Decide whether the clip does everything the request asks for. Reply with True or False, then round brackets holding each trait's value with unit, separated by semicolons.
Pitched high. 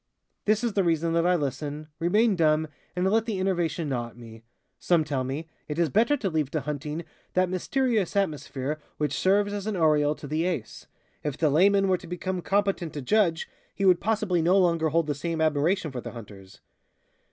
False (165 Hz)